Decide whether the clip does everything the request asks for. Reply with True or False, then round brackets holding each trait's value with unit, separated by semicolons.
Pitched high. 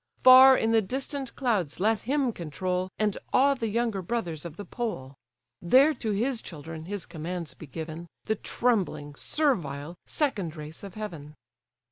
True (200 Hz)